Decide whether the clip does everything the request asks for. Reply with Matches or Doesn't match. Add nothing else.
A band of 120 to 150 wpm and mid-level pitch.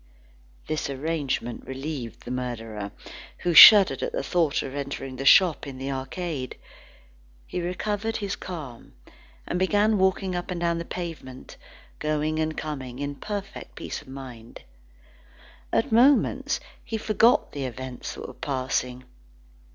Matches